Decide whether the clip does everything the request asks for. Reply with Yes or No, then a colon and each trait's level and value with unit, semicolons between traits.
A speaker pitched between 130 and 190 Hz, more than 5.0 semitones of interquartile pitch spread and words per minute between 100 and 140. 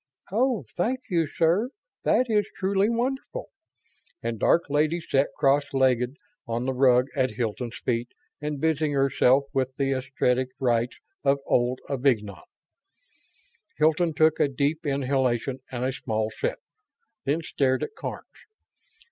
No: medium, 140 Hz; average, 4.2 semitones; slow, 135 wpm